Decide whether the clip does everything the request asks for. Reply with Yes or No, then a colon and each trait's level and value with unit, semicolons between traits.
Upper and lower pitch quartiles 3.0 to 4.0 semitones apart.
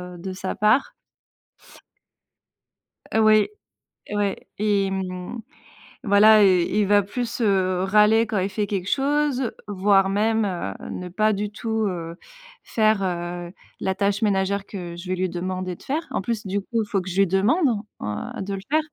No: narrow, 2.6 semitones